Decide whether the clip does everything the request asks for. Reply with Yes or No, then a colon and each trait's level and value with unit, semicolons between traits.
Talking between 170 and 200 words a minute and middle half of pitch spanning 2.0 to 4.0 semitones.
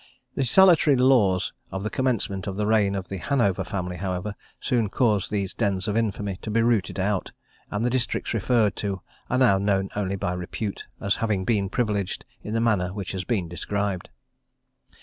Yes: average, 185 wpm; average, 3.0 semitones